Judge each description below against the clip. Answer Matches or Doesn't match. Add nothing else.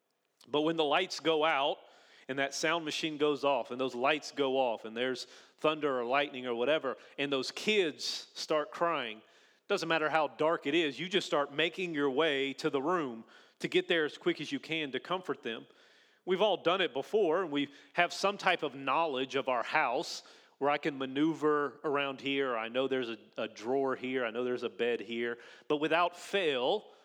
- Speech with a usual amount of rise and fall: Matches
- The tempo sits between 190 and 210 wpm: Matches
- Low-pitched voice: Doesn't match